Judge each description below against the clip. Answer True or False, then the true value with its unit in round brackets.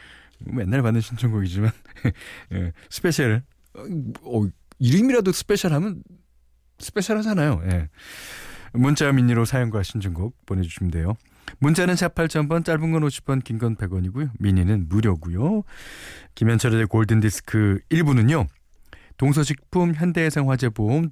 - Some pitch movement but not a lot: False (7.3 semitones)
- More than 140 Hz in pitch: False (115 Hz)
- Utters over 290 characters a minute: False (280 characters per minute)